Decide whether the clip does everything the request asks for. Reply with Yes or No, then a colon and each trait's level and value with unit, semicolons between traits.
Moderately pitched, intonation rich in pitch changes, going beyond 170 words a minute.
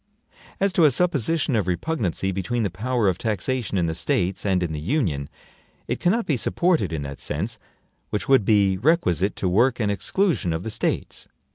No: low, 105 Hz; wide, 7.3 semitones; average, 185 wpm